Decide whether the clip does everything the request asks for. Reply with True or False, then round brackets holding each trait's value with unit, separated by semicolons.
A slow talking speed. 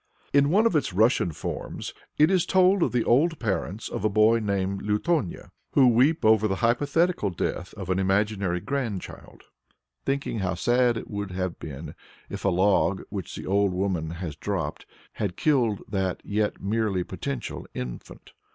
False (170 wpm)